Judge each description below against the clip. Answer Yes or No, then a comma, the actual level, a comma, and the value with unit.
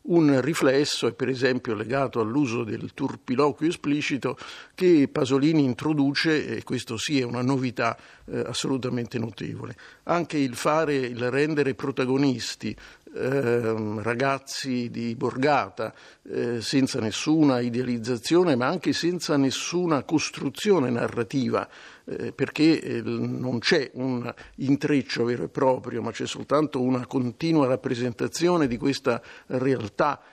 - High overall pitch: No, low, 135 Hz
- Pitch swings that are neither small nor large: Yes, average, 3.4 semitones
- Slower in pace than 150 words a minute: Yes, average, 120 wpm